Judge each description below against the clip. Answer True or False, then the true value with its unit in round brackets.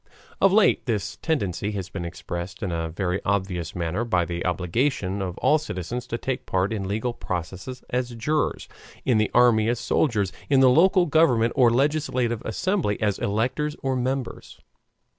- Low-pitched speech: True (115 Hz)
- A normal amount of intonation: False (5.8 semitones)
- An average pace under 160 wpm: False (165 wpm)